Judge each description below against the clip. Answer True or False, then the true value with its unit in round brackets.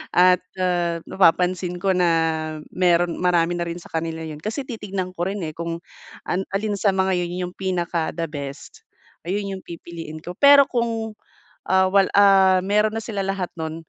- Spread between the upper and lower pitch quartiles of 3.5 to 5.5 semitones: False (2.6 semitones)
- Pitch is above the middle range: False (180 Hz)